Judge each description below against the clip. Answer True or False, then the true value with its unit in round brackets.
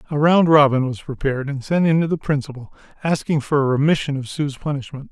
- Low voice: False (145 Hz)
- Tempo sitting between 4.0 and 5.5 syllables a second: False (6.1 syllables/s)